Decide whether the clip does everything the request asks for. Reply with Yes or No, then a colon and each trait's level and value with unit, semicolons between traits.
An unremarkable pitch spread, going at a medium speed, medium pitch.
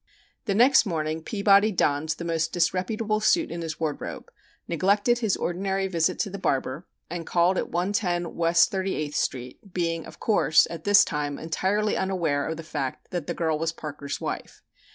Yes: average, 3.8 semitones; average, 175 wpm; medium, 170 Hz